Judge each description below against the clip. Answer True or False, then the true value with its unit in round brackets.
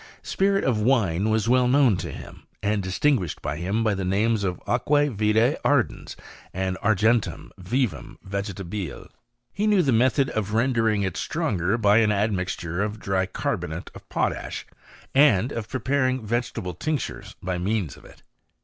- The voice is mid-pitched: False (110 Hz)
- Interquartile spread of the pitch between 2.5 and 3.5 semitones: False (4.6 semitones)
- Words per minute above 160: False (155 wpm)